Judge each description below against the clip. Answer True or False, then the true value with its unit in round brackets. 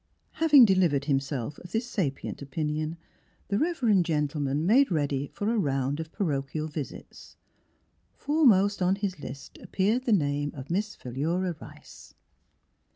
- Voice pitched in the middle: True (165 Hz)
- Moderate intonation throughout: False (6.1 semitones)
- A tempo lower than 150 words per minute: True (140 wpm)